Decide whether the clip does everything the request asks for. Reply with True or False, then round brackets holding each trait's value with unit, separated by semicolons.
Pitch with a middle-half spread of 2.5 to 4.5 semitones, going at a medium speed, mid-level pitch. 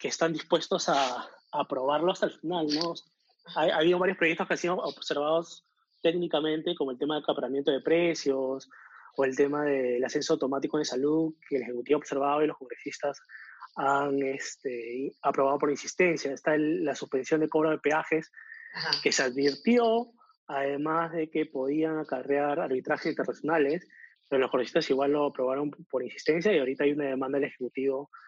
True (3.0 semitones; 170 wpm; 150 Hz)